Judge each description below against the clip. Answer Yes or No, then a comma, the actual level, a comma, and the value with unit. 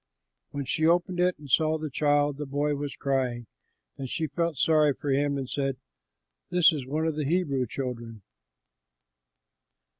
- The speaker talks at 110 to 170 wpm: Yes, average, 160 wpm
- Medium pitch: Yes, medium, 145 Hz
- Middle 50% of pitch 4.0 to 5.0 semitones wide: No, average, 2.7 semitones